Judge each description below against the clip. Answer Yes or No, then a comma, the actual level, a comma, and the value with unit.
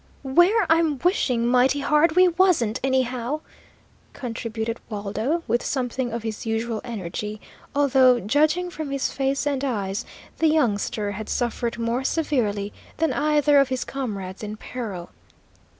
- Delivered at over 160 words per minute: No, slow, 135 wpm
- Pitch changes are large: No, average, 4.7 semitones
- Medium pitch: No, very high, 255 Hz